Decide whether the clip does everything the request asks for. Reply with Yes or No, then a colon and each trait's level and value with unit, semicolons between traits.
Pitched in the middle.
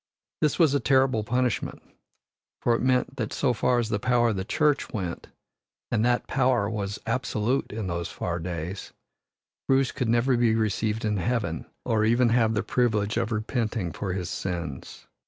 No: low, 115 Hz